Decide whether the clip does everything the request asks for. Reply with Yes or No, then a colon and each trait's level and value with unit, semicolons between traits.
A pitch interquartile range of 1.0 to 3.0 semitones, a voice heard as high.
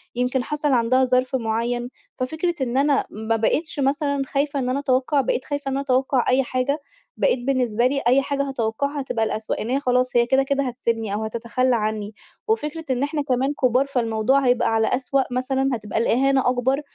Yes: narrow, 2.6 semitones; very high, 255 Hz